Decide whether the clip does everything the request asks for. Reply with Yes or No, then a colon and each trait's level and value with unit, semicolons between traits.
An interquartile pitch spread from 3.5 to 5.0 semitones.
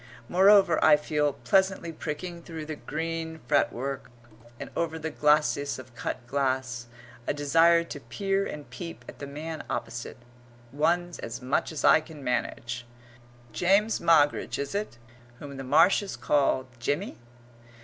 Yes: average, 3.8 semitones